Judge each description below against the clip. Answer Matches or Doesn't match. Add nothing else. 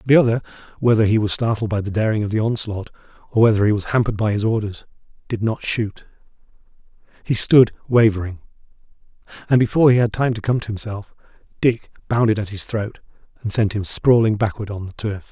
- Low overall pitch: Matches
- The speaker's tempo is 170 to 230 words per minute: Matches